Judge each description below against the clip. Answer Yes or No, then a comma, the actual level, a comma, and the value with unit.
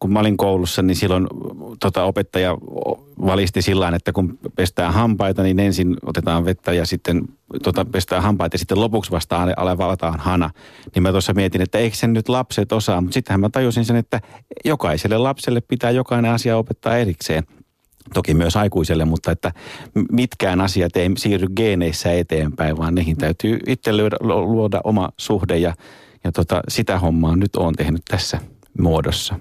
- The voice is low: Yes, very low, 95 Hz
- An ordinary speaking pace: No, fast, 165 wpm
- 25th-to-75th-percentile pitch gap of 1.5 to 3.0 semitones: No, average, 3.8 semitones